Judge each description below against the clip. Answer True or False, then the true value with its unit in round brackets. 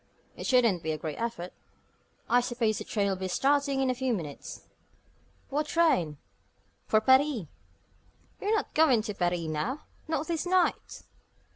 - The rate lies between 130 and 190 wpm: True (155 wpm)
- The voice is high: True (240 Hz)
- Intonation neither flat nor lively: False (7.6 semitones)